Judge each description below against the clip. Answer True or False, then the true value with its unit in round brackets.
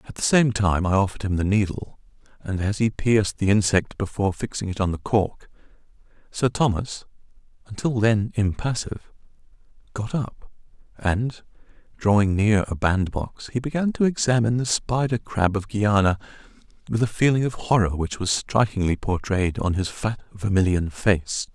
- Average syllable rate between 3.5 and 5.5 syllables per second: True (5.0 syllables/s)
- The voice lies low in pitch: True (105 Hz)